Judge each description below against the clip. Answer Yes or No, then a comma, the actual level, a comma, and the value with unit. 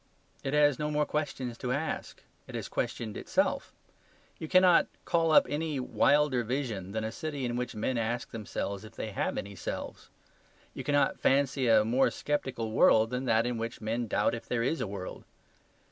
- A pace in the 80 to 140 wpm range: No, average, 185 wpm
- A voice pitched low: Yes, low, 125 Hz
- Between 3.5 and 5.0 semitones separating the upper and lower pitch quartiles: Yes, average, 4.7 semitones